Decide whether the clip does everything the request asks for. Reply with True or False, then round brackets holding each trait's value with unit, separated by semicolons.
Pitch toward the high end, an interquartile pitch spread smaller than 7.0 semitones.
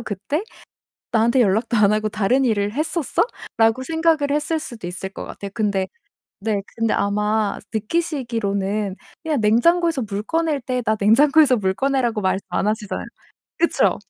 True (225 Hz; 5.6 semitones)